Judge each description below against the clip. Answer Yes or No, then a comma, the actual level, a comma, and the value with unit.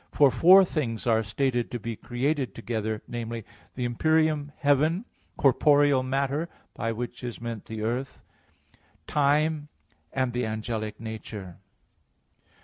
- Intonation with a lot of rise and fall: No, average, 4.2 semitones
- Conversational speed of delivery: No, slow, 125 wpm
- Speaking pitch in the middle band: No, low, 125 Hz